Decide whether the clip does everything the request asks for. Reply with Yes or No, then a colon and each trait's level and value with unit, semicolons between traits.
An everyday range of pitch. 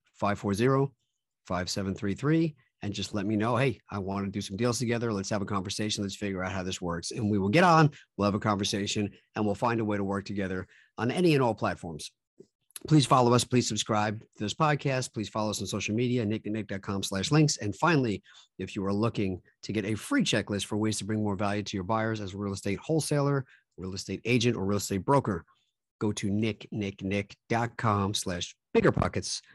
Yes: average, 3.2 semitones